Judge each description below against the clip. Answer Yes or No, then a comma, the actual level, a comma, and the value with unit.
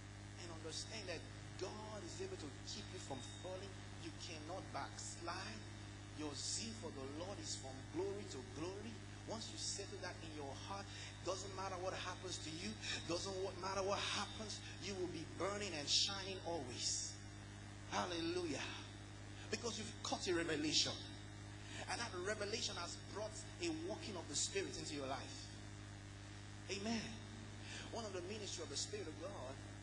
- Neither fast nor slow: Yes, average, 155 wpm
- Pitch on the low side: Yes, low, 105 Hz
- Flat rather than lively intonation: Yes, narrow, 1.0 semitones